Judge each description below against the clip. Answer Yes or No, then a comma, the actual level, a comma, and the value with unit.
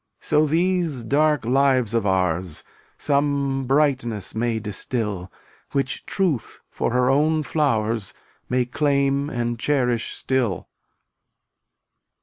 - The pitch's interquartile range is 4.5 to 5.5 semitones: No, average, 4.1 semitones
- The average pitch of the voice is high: No, low, 130 Hz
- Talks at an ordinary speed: No, slow, 105 wpm